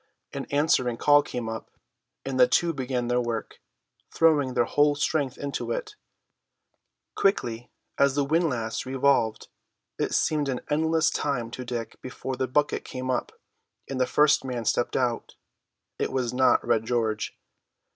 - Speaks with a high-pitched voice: No, low, 130 Hz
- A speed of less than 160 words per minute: Yes, average, 150 wpm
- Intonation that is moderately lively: Yes, average, 3.2 semitones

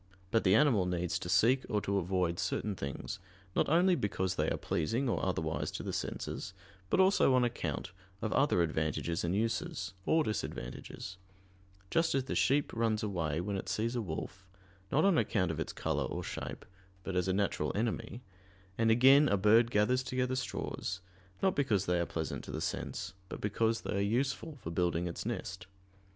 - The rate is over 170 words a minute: Yes, average, 185 wpm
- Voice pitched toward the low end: Yes, low, 105 Hz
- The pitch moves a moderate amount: No, wide, 5.7 semitones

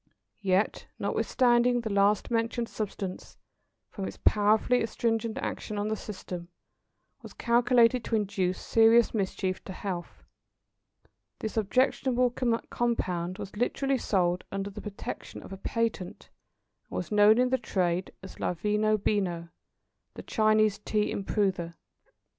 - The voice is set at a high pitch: Yes, high, 210 Hz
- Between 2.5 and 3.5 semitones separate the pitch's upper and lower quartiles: Yes, average, 3.2 semitones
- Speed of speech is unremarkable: No, slow, 130 wpm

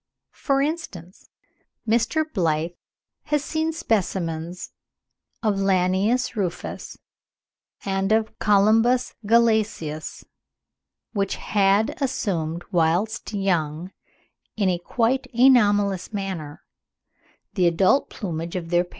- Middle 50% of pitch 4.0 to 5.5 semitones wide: Yes, average, 4.5 semitones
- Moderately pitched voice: No, high, 195 Hz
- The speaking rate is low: Yes, slow, 95 wpm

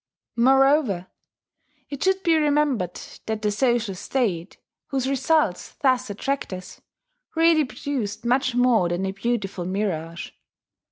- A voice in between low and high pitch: No, high, 240 Hz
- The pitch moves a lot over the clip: Yes, wide, 6.0 semitones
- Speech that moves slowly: Yes, slow, 120 wpm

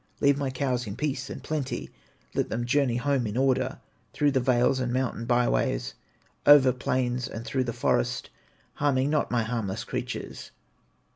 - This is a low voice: Yes, low, 125 Hz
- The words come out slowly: No, average, 165 wpm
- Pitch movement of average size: No, narrow, 2.3 semitones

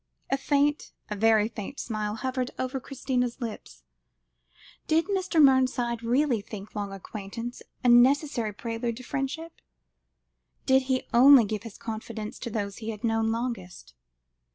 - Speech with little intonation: No, average, 3.4 semitones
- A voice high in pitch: Yes, high, 235 Hz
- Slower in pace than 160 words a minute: Yes, average, 140 wpm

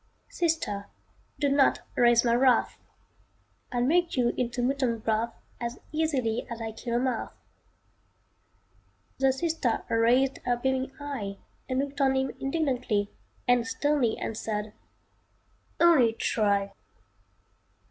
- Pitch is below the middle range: No, high, 245 Hz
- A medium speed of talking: No, slow, 115 wpm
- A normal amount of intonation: Yes, average, 3.1 semitones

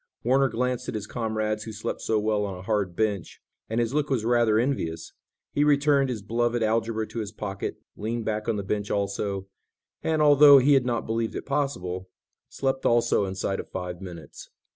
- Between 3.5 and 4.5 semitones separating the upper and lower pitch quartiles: Yes, average, 3.8 semitones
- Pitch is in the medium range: No, low, 110 Hz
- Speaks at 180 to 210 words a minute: Yes, average, 190 wpm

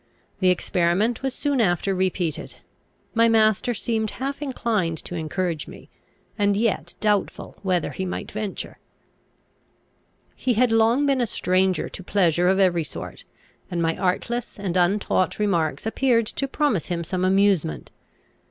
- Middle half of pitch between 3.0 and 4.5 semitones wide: Yes, average, 4.2 semitones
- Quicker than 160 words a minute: No, average, 145 wpm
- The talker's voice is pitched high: Yes, high, 195 Hz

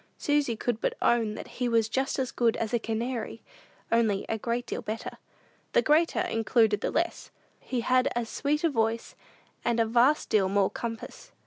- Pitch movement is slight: Yes, narrow, 2.3 semitones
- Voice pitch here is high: Yes, high, 235 Hz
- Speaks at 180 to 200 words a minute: Yes, average, 185 wpm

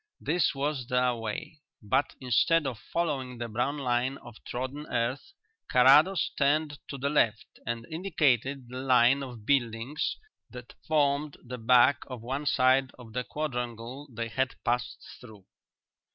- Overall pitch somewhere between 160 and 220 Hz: No, low, 130 Hz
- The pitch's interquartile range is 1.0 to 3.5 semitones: Yes, average, 2.9 semitones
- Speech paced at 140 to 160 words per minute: Yes, average, 145 wpm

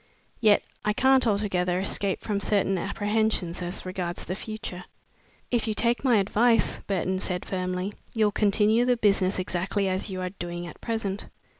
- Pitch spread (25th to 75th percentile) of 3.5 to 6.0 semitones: No, average, 3.0 semitones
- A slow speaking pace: No, average, 160 wpm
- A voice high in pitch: Yes, high, 200 Hz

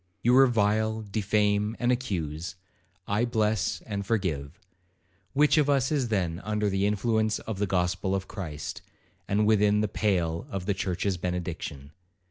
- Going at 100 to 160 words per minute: Yes, average, 140 wpm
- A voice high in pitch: No, low, 105 Hz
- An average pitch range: Yes, average, 3.2 semitones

